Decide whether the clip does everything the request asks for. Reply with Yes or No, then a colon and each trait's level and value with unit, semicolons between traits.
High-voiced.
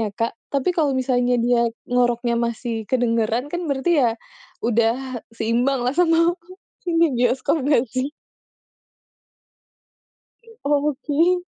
Yes: very high, 255 Hz